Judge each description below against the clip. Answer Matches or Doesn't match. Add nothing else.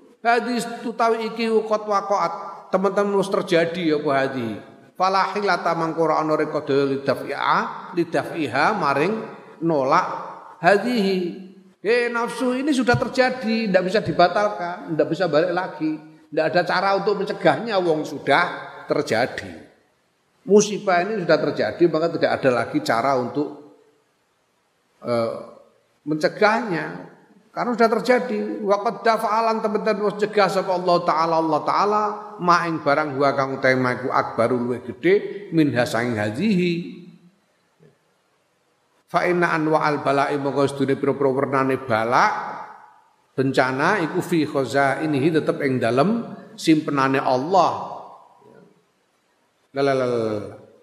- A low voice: Doesn't match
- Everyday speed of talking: Matches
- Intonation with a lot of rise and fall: Matches